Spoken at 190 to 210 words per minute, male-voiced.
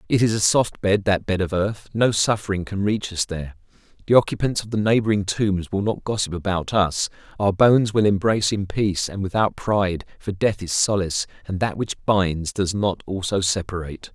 Yes: average, 200 wpm; male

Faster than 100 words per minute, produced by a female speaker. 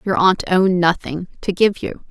Yes: average, 200 wpm; female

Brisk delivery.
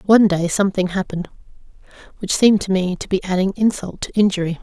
No: average, 180 wpm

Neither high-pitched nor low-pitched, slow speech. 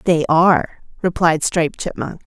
Yes: medium, 165 Hz; slow, 130 wpm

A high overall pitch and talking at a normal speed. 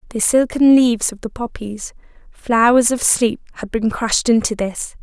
Yes: high, 230 Hz; average, 145 wpm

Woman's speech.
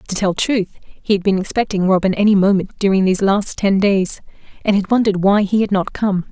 Yes: female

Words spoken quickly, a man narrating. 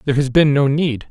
Yes: fast, 270 wpm; male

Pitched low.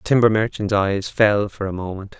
Yes: low, 105 Hz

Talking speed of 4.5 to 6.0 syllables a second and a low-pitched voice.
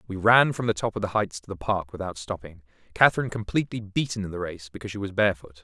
No: 7.2 syllables/s; low, 105 Hz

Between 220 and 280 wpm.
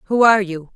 Yes: fast, 240 wpm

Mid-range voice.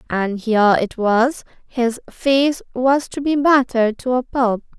No: high, 245 Hz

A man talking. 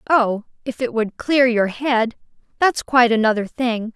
No: female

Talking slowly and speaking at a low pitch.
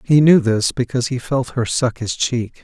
No: fast, 230 wpm; low, 120 Hz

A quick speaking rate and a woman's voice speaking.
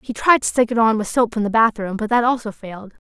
Yes: fast, 295 wpm; female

